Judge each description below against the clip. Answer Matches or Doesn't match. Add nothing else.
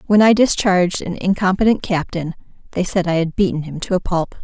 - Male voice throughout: Doesn't match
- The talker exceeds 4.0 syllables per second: Matches